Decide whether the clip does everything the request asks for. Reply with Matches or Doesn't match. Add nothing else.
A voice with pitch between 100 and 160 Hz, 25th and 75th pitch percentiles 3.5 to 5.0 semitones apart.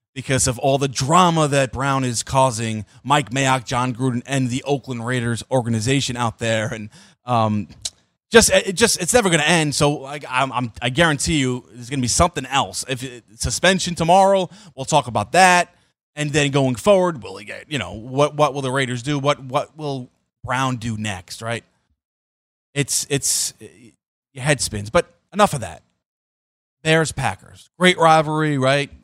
Matches